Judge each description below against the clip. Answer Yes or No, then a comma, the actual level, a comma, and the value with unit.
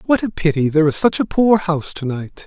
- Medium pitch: Yes, medium, 170 Hz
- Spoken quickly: Yes, fast, 245 wpm